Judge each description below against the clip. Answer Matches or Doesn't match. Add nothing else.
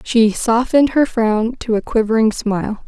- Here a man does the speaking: Doesn't match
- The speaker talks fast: Doesn't match